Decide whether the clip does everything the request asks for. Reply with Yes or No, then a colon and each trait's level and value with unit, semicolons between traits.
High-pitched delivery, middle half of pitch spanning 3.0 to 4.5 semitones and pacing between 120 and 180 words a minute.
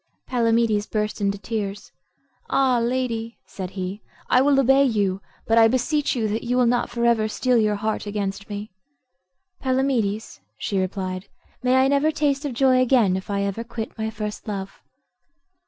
Yes: high, 225 Hz; average, 3.8 semitones; average, 170 wpm